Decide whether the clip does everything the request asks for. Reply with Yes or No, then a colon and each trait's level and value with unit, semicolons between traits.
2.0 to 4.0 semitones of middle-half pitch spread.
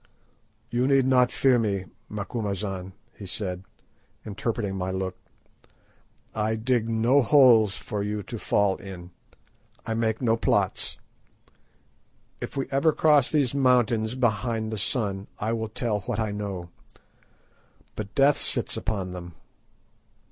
Yes: average, 3.6 semitones